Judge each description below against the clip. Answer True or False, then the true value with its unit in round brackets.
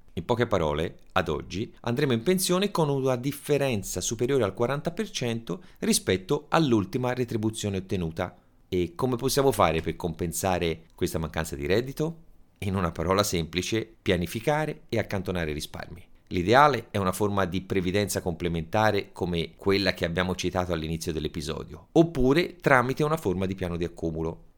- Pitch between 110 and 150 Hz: False (100 Hz)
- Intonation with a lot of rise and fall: True (6.4 semitones)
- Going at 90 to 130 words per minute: False (140 wpm)